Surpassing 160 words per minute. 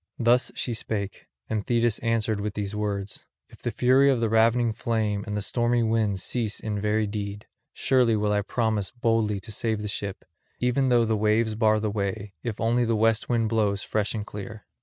Yes: average, 200 wpm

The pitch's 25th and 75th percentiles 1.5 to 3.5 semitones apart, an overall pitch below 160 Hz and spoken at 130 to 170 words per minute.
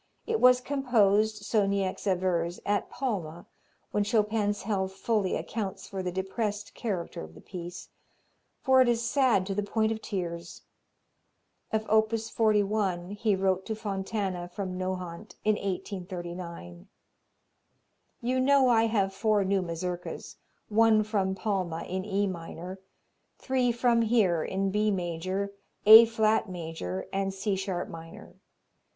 No: average, 3.1 semitones; high, 200 Hz; slow, 135 wpm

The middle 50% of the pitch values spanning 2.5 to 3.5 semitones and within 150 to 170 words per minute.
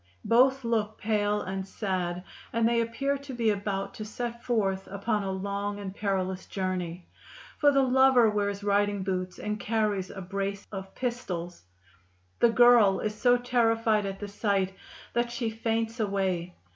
Yes: average, 3.2 semitones; average, 160 wpm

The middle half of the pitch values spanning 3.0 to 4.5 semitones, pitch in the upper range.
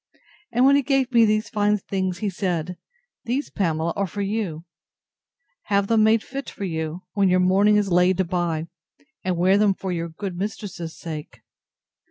Yes: average, 3.3 semitones; high, 195 Hz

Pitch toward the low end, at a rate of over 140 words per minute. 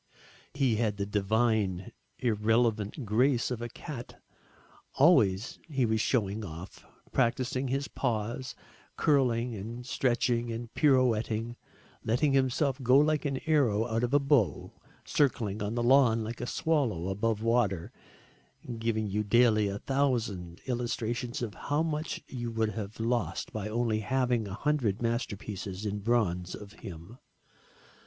No: low, 115 Hz; slow, 135 wpm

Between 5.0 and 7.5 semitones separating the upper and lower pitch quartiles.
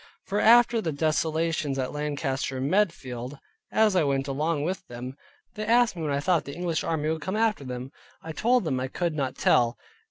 Yes: wide, 5.4 semitones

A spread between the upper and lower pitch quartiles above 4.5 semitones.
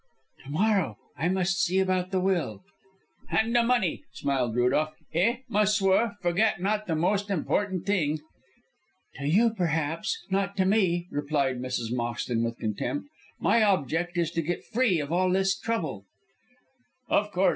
Yes: average, 5.3 semitones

